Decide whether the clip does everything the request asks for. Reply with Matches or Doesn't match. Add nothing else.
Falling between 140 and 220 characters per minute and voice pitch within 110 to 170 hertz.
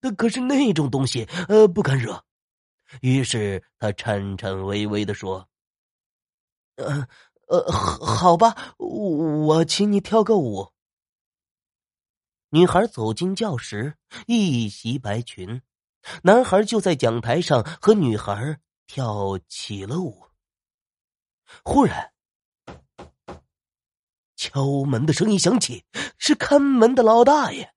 Matches